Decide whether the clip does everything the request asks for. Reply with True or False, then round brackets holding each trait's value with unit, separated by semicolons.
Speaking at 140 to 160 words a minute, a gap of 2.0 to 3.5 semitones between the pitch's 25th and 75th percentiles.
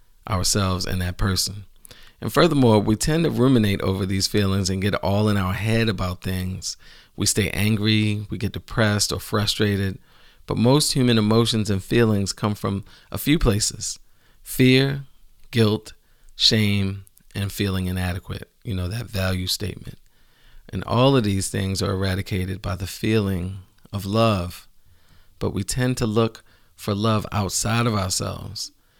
True (150 wpm; 2.8 semitones)